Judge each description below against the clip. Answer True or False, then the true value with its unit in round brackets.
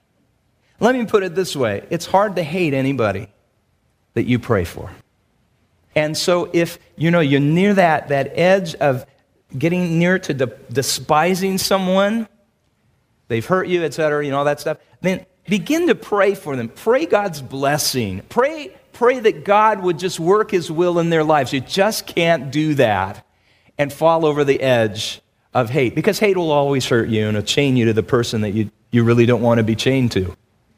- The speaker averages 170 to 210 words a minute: True (190 wpm)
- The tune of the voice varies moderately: False (7.3 semitones)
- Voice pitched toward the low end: False (145 Hz)